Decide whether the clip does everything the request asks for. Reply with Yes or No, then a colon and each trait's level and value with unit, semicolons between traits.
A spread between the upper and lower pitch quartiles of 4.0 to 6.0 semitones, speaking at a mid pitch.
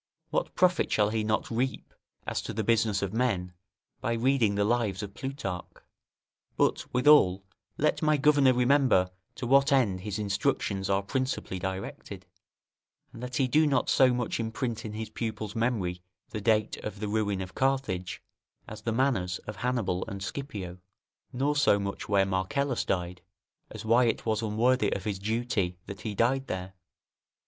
No: average, 4.5 semitones; low, 110 Hz